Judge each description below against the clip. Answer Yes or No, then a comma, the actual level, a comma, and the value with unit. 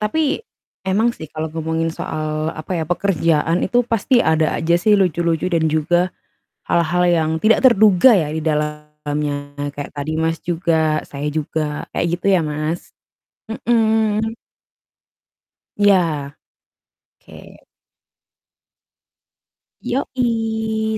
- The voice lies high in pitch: No, medium, 165 Hz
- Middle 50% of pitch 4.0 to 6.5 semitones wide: Yes, average, 5.2 semitones